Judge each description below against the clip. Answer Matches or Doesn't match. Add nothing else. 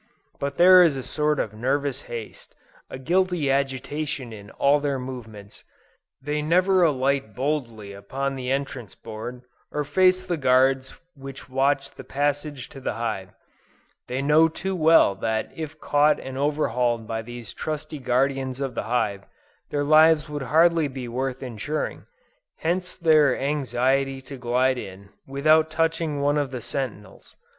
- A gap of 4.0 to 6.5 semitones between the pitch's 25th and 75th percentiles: Doesn't match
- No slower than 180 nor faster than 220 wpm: Doesn't match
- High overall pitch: Doesn't match